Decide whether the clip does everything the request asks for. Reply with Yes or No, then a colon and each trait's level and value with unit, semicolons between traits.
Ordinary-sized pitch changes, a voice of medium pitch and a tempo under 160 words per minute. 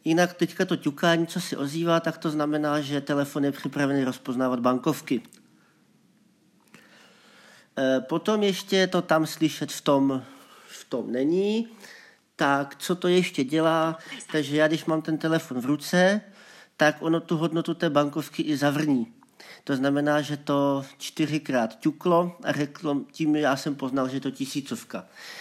Yes: average, 3.1 semitones; medium, 155 Hz; average, 150 wpm